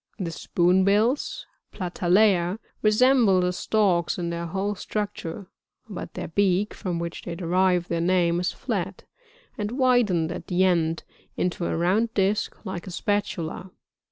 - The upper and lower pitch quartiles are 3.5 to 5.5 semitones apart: No, average, 3.1 semitones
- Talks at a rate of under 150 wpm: No, average, 165 wpm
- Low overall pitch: No, medium, 185 Hz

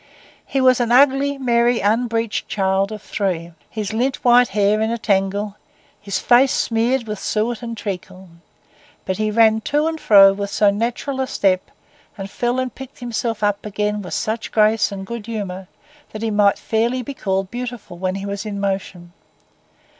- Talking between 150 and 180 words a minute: Yes, average, 175 wpm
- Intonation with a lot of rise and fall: No, average, 3.3 semitones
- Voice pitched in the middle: No, high, 215 Hz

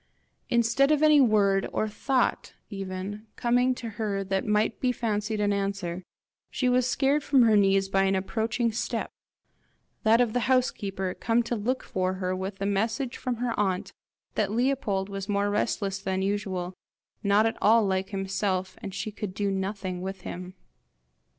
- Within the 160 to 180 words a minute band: Yes, average, 170 wpm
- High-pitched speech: Yes, high, 205 Hz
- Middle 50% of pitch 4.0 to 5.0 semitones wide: No, average, 3.3 semitones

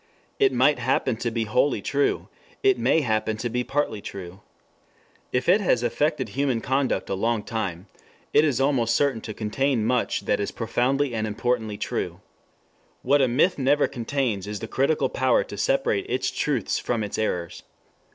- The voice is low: Yes, low, 125 Hz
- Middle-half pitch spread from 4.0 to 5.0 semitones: Yes, average, 4.4 semitones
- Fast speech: No, average, 170 wpm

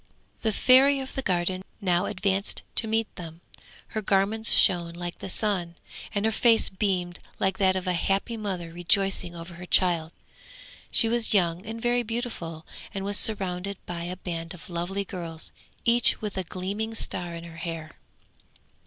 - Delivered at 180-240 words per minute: No, average, 170 wpm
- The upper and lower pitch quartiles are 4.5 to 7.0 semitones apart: No, average, 3.7 semitones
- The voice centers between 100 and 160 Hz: No, high, 190 Hz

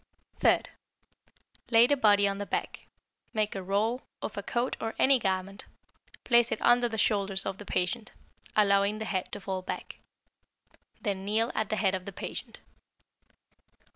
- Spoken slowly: No, average, 165 wpm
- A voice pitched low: No, high, 205 Hz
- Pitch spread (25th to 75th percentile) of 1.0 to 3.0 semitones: Yes, narrow, 2.6 semitones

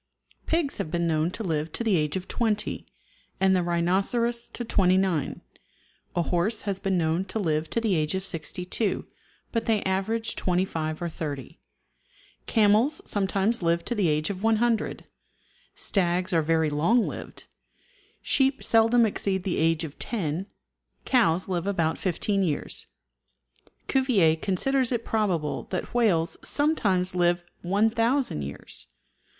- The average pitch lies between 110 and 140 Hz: No, high, 190 Hz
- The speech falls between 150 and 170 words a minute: No, average, 140 wpm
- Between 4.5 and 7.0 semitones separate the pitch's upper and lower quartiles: Yes, average, 5.1 semitones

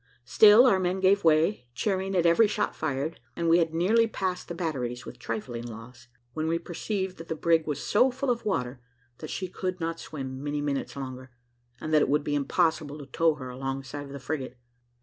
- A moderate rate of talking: No, fast, 210 wpm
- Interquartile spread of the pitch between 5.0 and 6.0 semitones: Yes, wide, 5.4 semitones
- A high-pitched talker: No, medium, 160 Hz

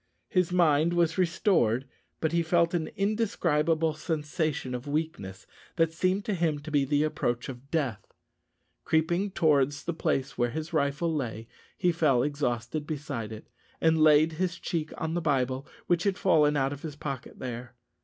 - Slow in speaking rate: No, average, 165 wpm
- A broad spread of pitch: No, average, 3.5 semitones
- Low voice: No, medium, 155 Hz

